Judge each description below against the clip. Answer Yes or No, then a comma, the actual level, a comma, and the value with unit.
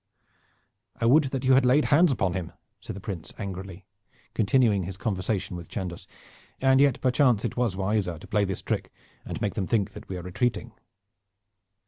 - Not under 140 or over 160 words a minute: No, average, 180 wpm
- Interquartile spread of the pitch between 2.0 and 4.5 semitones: No, average, 5.2 semitones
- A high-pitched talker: No, low, 105 Hz